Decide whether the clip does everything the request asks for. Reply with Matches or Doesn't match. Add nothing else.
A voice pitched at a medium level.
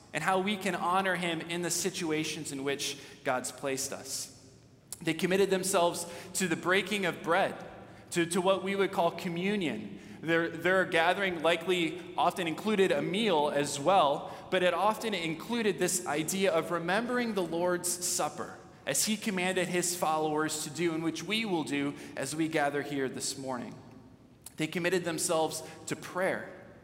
Matches